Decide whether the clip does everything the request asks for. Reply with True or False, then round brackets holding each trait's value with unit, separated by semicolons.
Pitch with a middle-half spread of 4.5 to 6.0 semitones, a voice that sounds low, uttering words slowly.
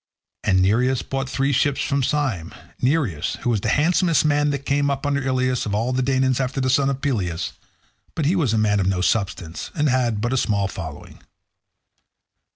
False (5.1 semitones; 130 Hz; 185 wpm)